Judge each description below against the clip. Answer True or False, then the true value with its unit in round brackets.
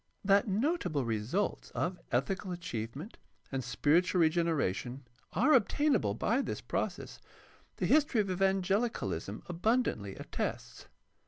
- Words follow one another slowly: True (105 wpm)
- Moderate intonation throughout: False (8.4 semitones)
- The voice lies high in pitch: False (180 Hz)